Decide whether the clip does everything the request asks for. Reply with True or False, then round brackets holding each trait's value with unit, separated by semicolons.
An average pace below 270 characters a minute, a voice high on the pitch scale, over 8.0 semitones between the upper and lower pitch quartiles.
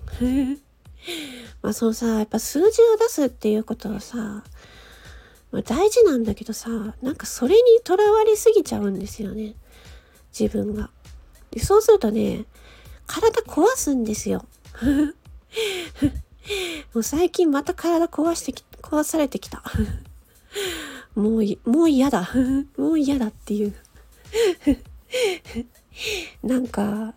True (225 characters per minute; 275 Hz; 8.6 semitones)